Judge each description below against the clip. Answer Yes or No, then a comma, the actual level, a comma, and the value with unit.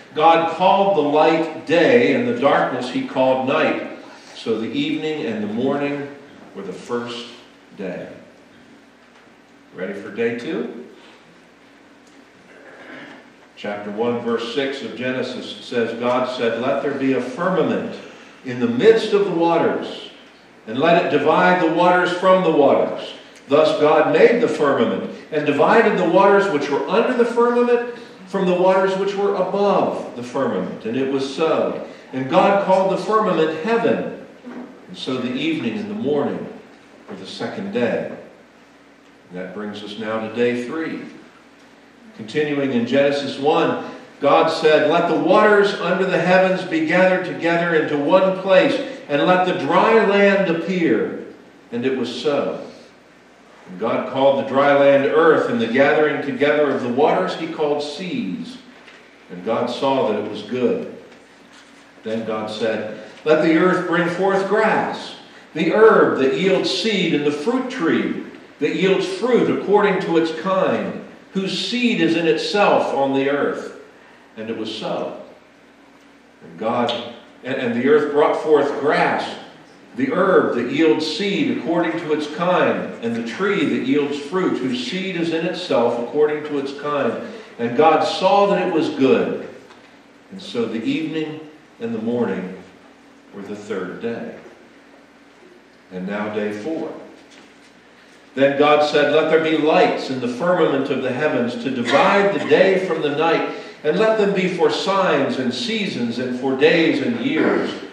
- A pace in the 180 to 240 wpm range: No, average, 155 wpm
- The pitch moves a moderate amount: No, wide, 7.4 semitones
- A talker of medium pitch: Yes, medium, 170 Hz